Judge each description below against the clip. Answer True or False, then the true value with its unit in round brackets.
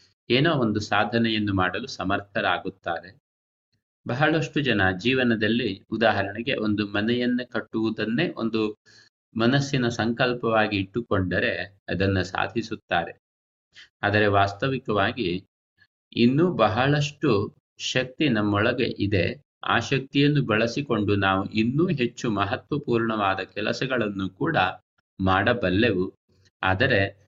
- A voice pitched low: True (110 Hz)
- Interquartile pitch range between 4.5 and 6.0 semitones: False (3.7 semitones)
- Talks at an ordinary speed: True (80 wpm)